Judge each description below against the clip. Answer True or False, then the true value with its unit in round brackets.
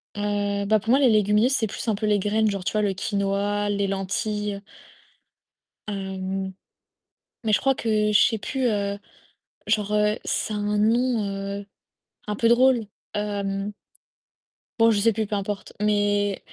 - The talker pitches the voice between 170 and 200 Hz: False (210 Hz)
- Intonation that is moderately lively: False (1.4 semitones)